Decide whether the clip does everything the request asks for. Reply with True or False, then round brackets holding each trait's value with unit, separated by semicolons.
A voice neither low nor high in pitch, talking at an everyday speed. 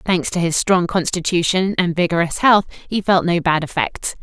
True (175 Hz; 185 wpm)